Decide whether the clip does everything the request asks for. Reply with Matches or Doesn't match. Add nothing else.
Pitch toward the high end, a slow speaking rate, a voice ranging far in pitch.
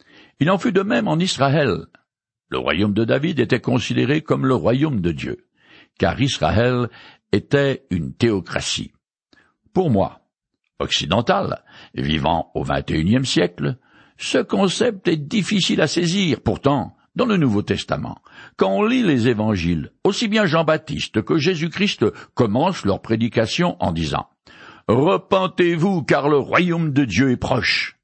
Doesn't match